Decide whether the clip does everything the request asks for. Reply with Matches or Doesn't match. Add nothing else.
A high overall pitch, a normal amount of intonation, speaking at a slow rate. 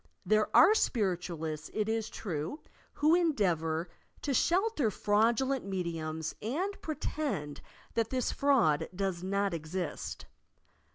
Doesn't match